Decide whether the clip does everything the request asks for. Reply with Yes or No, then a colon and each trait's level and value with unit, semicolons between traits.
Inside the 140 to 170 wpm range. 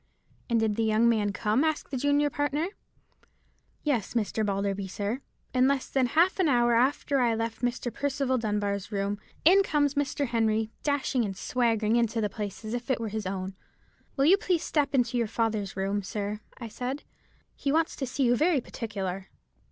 No: average, 190 wpm